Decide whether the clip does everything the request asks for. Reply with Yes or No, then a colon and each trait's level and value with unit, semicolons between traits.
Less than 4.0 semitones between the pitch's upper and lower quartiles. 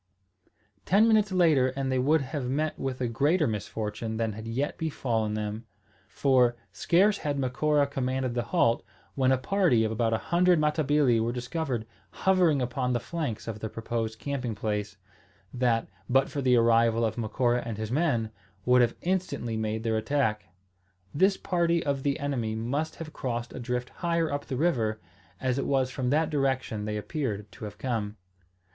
No: average, 4.5 semitones